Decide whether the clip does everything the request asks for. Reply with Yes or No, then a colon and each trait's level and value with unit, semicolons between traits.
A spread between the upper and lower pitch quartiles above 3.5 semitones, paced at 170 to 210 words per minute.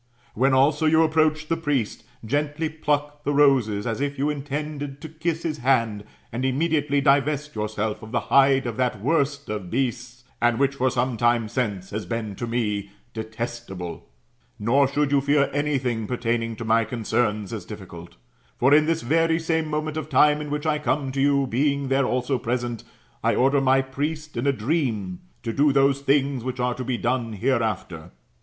Yes: average, 4.0 semitones; average, 185 wpm